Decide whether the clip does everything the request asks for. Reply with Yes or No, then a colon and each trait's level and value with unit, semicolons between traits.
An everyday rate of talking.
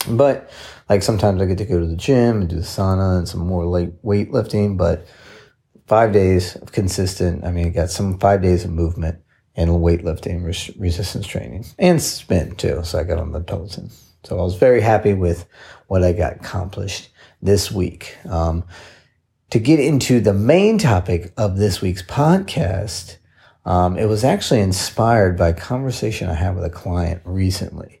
Yes: average, 185 wpm